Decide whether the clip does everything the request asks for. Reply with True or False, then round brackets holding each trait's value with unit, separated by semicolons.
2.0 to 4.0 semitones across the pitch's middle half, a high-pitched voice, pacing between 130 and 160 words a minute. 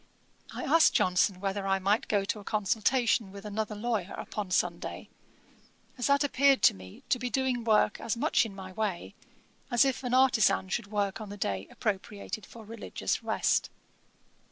False (3.7 semitones; 210 Hz; 175 wpm)